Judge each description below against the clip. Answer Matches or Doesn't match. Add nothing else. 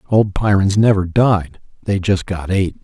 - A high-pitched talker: Doesn't match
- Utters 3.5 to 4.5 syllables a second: Matches